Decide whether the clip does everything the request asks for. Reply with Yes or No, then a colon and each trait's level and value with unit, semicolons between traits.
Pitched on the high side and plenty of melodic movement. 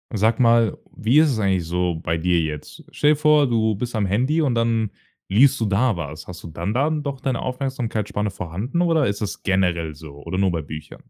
No: low, 110 Hz; wide, 6.4 semitones